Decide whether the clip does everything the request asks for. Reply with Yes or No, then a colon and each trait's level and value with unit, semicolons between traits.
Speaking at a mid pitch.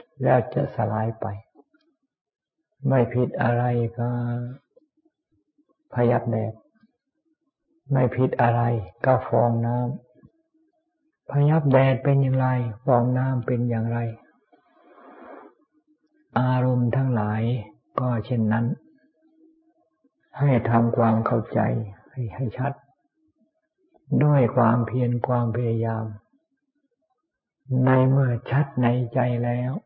No: low, 130 Hz